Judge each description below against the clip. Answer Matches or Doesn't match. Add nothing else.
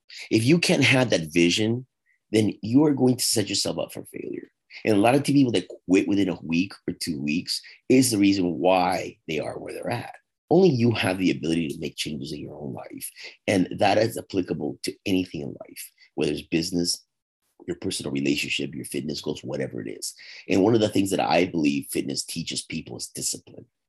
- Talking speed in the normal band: Doesn't match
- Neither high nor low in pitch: Doesn't match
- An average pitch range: Doesn't match